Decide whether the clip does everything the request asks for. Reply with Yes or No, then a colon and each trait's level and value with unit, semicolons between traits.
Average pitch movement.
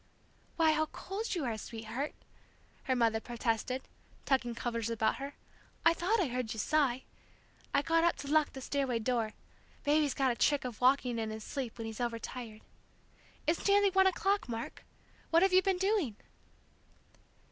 No: wide, 6.0 semitones